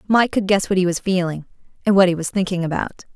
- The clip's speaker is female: Yes, female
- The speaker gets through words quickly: Yes, fast, 250 wpm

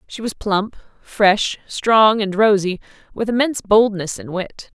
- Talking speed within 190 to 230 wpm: No, average, 150 wpm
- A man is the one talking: No, female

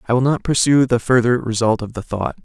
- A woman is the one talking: No, male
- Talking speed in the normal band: No, fast, 245 wpm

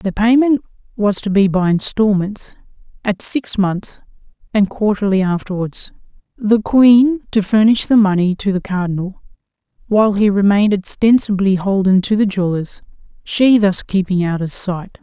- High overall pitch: Yes, high, 200 Hz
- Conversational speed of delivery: Yes, average, 145 wpm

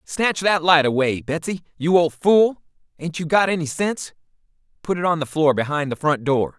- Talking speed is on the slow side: No, average, 200 wpm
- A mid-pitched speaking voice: Yes, medium, 160 Hz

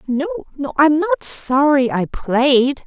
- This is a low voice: No, very high, 270 Hz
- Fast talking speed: No, average, 145 wpm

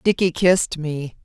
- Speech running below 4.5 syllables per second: No, 4.6 syllables/s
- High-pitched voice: No, medium, 165 Hz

